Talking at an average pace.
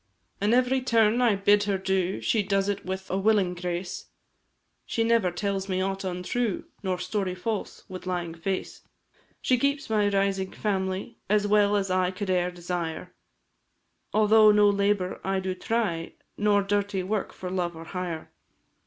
Yes: average, 160 wpm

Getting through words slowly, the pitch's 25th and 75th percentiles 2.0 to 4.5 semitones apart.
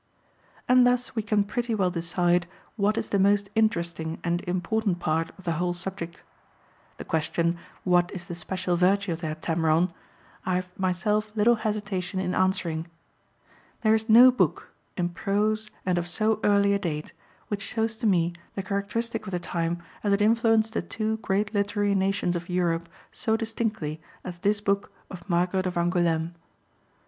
No: average, 170 wpm; average, 3.5 semitones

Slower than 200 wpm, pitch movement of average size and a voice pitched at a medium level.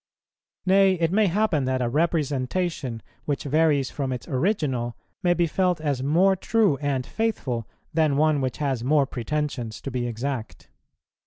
Yes: average, 155 wpm; average, 5.0 semitones; medium, 145 Hz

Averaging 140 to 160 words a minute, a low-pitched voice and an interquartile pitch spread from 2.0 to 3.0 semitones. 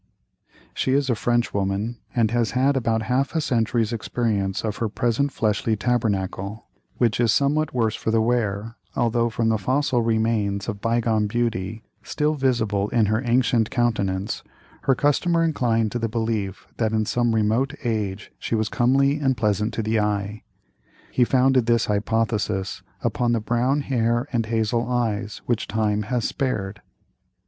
Yes: average, 155 wpm; low, 115 Hz; narrow, 2.5 semitones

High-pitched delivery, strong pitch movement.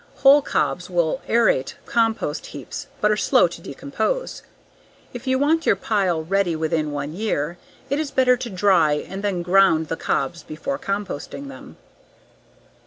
Yes: high, 195 Hz; wide, 7.5 semitones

